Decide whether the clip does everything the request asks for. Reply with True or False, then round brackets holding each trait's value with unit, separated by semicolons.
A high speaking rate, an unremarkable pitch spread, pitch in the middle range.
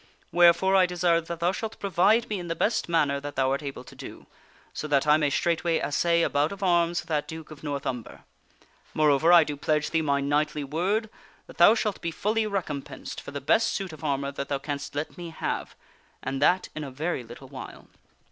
True (225 wpm; 3.6 semitones; 160 Hz)